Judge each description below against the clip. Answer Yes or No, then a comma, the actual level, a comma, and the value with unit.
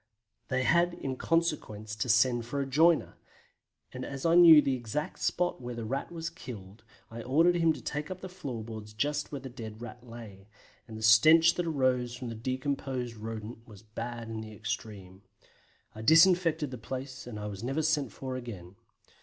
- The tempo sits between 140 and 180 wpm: No, average, 190 wpm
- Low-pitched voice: Yes, low, 125 Hz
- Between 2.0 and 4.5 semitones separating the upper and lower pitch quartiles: No, average, 5.2 semitones